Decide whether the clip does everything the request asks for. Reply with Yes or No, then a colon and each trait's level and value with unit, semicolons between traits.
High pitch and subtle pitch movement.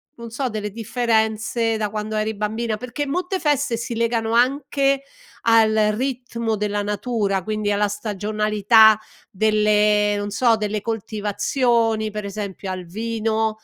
Yes: high, 220 Hz; narrow, 1.9 semitones